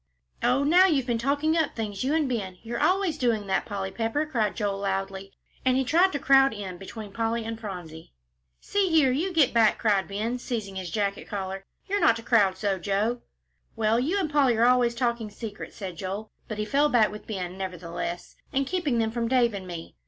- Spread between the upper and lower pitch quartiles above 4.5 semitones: Yes, average, 5.2 semitones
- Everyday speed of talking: No, fast, 210 wpm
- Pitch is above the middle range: Yes, high, 225 Hz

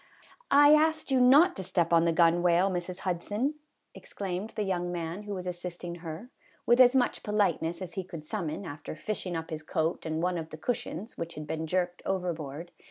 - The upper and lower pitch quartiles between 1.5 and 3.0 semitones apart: No, average, 3.9 semitones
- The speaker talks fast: Yes, fast, 215 wpm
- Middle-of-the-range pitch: Yes, medium, 180 Hz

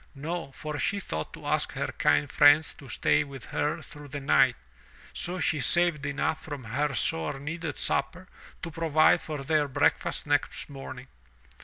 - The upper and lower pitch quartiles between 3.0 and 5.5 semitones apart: No, narrow, 2.6 semitones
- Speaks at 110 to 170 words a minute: Yes, average, 165 wpm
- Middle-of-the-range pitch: Yes, medium, 145 Hz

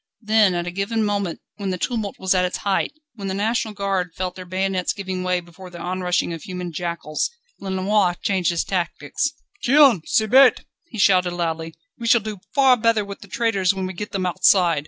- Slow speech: No, fast, 205 wpm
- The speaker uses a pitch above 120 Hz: Yes, high, 190 Hz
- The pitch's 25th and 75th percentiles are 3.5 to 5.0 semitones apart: No, average, 2.8 semitones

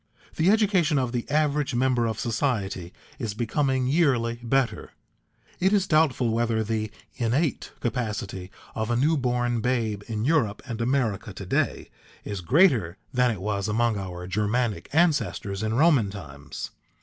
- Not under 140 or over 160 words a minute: Yes, average, 150 wpm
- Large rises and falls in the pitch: No, average, 4.6 semitones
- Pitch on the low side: Yes, low, 120 Hz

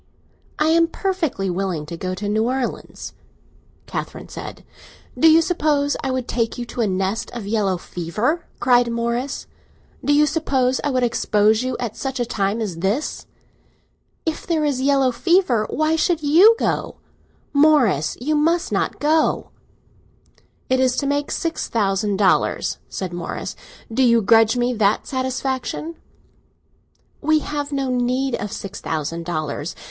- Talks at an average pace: Yes, average, 155 wpm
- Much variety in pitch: Yes, wide, 5.9 semitones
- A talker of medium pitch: No, very high, 250 Hz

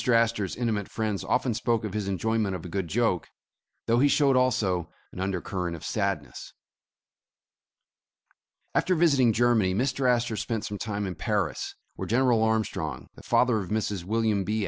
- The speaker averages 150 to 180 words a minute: Yes, average, 165 wpm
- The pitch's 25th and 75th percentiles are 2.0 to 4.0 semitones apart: Yes, average, 3.7 semitones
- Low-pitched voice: Yes, low, 110 Hz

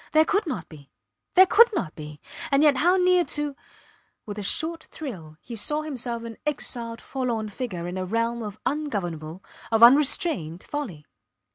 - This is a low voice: No, high, 235 Hz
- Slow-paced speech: No, average, 165 wpm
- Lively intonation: Yes, wide, 8.1 semitones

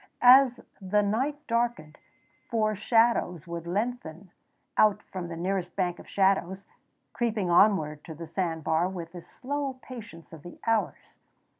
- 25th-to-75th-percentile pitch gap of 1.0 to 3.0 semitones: No, average, 5.0 semitones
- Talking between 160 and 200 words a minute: No, average, 145 wpm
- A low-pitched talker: No, high, 190 Hz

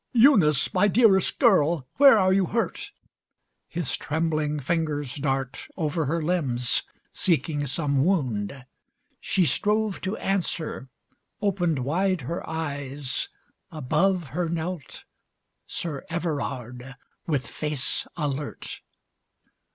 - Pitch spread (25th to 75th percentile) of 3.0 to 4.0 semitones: No, average, 4.7 semitones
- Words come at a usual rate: No, slow, 105 wpm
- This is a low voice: No, medium, 155 Hz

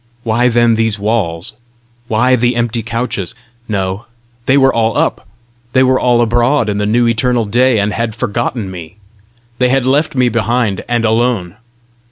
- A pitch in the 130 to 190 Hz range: No, low, 115 Hz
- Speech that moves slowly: No, average, 165 wpm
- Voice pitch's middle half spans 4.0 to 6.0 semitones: No, narrow, 2.6 semitones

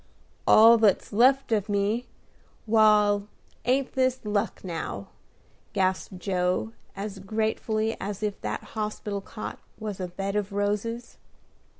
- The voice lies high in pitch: Yes, high, 210 Hz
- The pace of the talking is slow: Yes, slow, 120 wpm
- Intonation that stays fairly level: Yes, narrow, 2.0 semitones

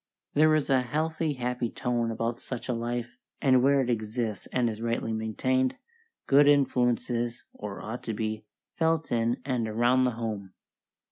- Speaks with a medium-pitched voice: No, low, 120 Hz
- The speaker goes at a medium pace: Yes, average, 165 wpm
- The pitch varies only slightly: Yes, narrow, 2.3 semitones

